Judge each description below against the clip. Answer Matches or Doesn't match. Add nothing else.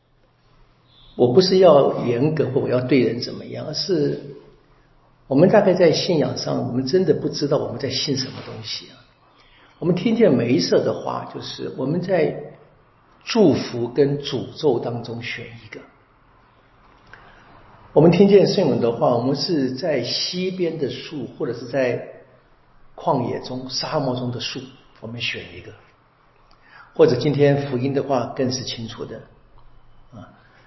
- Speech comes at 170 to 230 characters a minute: Matches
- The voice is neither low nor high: Doesn't match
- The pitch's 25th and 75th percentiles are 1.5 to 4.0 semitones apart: Matches